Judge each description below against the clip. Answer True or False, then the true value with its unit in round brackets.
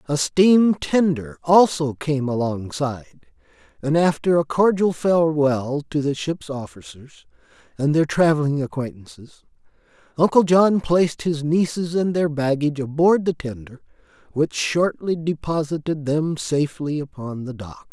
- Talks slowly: True (125 wpm)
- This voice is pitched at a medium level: True (150 Hz)